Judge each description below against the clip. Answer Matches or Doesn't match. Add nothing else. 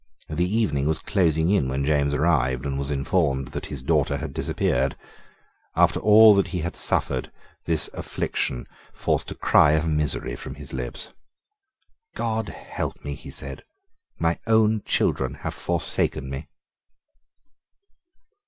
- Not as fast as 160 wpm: Matches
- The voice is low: Matches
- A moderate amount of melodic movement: Matches